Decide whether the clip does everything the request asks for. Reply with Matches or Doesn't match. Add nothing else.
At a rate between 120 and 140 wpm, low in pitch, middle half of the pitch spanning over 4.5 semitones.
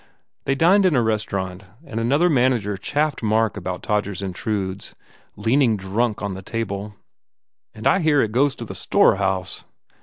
Doesn't match